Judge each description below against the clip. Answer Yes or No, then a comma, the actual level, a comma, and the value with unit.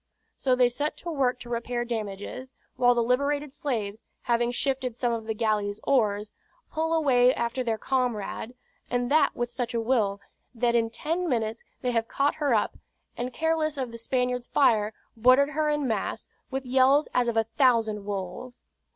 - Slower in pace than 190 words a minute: Yes, average, 175 wpm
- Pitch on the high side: Yes, high, 245 Hz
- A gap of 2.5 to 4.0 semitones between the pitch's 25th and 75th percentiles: Yes, average, 3.0 semitones